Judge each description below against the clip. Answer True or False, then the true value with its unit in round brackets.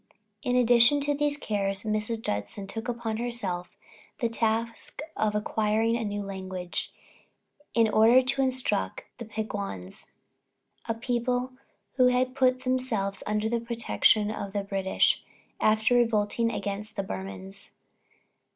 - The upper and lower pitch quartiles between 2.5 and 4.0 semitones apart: True (3.3 semitones)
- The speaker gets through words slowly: True (130 wpm)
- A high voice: True (220 Hz)